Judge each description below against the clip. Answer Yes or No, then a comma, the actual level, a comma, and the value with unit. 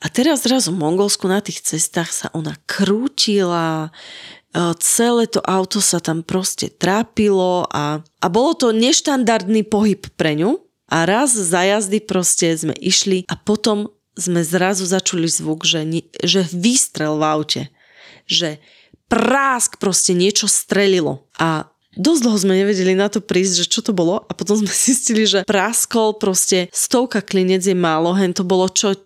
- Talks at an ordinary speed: Yes, average, 155 wpm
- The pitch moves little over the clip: No, average, 3.6 semitones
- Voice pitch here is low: No, high, 195 Hz